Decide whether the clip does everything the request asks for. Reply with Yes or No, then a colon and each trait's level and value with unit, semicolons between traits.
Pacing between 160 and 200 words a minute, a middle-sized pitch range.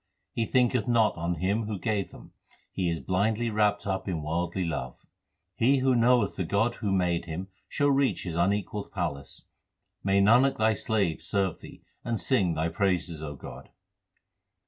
Yes: average, 170 wpm; average, 4.7 semitones